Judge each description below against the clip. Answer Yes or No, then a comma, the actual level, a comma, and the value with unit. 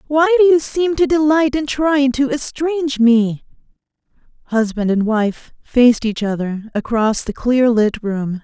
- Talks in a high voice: Yes, very high, 255 Hz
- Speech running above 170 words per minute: No, average, 155 wpm